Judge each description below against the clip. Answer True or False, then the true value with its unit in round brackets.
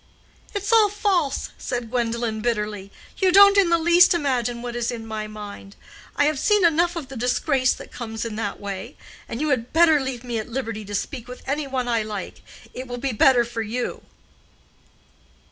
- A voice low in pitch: False (245 Hz)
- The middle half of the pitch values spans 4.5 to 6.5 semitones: True (5.3 semitones)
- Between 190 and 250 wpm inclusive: True (195 wpm)